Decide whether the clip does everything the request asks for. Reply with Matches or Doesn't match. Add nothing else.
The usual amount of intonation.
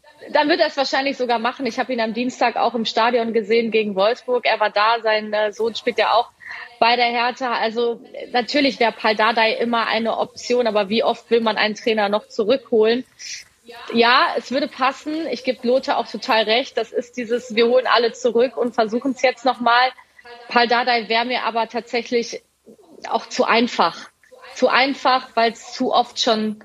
Doesn't match